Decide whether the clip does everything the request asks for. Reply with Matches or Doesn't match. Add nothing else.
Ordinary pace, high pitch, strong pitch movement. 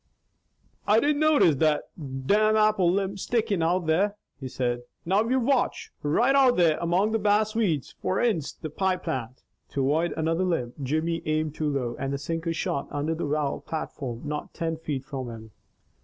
Doesn't match